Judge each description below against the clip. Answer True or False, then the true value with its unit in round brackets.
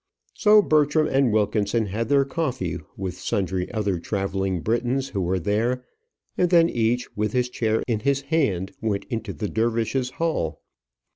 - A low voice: True (115 Hz)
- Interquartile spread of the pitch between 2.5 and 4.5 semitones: False (5.2 semitones)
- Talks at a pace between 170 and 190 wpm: False (155 wpm)